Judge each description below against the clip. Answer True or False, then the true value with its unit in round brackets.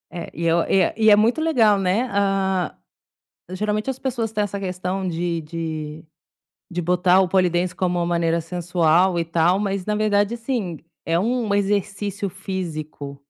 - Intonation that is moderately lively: True (3.3 semitones)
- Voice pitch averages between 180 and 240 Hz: True (185 Hz)